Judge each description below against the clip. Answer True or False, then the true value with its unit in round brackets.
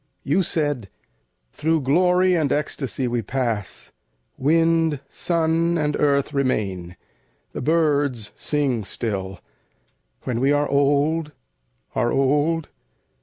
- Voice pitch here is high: False (145 Hz)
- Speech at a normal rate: False (105 wpm)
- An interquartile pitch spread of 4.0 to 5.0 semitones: True (4.4 semitones)